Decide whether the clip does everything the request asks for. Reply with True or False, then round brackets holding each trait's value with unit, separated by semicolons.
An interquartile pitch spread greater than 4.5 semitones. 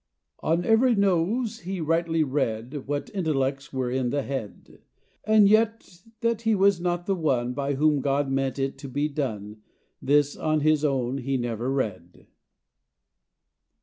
True (5.0 semitones)